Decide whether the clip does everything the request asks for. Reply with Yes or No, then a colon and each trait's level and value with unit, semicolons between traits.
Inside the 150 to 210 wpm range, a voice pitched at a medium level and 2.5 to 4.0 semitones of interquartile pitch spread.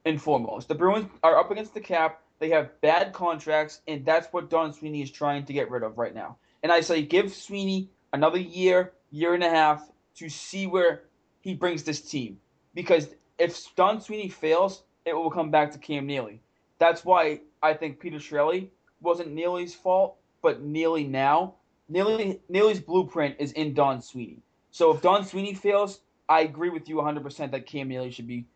Yes: average, 190 wpm; medium, 160 Hz; average, 3.6 semitones